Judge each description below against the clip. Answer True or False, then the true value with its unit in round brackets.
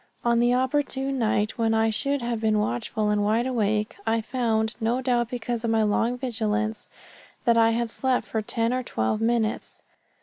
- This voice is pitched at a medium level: False (230 Hz)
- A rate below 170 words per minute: False (180 wpm)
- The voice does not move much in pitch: True (2.0 semitones)